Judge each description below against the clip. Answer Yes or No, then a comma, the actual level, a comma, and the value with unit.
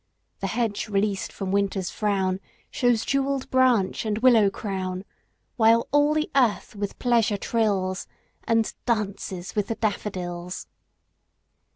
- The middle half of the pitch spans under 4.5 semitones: Yes, average, 3.3 semitones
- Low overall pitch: No, high, 210 Hz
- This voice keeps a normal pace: No, slow, 120 wpm